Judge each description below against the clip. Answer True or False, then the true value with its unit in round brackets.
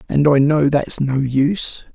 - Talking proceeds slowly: False (185 wpm)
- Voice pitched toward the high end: False (145 Hz)